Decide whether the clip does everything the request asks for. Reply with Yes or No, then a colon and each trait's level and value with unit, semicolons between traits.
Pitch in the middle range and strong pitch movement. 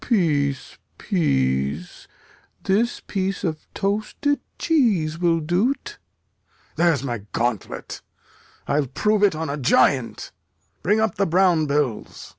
Yes: medium, 165 Hz; wide, 6.3 semitones